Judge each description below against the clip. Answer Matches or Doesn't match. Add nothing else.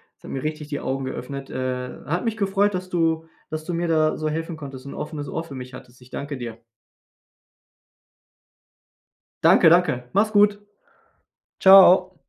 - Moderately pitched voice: Matches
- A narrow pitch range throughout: Doesn't match